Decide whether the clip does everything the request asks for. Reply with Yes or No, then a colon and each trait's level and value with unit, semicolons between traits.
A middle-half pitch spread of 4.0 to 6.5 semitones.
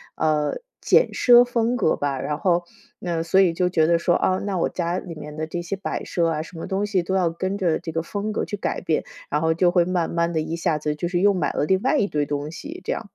No: average, 3.1 semitones